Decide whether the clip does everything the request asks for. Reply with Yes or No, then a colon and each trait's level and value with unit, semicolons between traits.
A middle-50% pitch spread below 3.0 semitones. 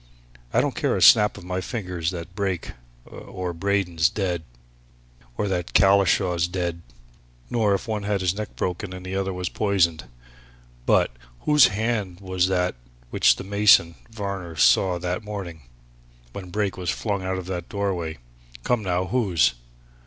Yes: narrow, 2.4 semitones